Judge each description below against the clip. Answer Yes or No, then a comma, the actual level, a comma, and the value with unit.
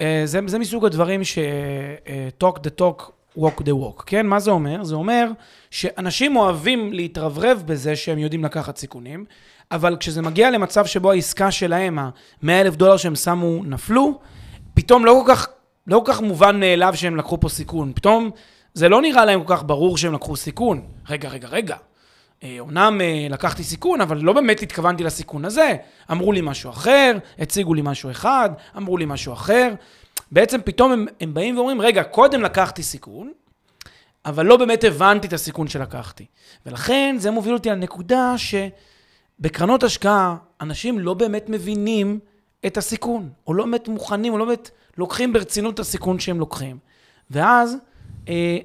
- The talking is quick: Yes, fast, 160 wpm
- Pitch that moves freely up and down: Yes, wide, 5.8 semitones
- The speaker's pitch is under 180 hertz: No, medium, 185 Hz